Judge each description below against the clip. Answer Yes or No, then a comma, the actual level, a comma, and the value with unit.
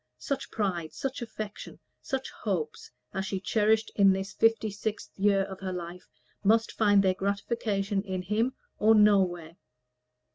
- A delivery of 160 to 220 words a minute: No, average, 145 wpm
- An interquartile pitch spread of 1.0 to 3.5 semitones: Yes, narrow, 2.4 semitones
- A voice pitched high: Yes, high, 200 Hz